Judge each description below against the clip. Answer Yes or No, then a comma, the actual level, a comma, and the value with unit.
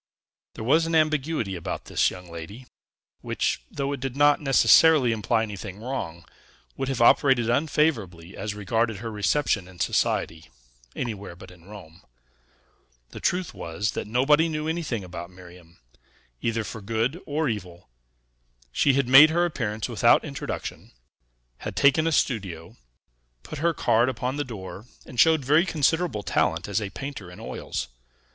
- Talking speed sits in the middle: Yes, average, 150 wpm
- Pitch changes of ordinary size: No, wide, 7.0 semitones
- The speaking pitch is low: Yes, low, 115 Hz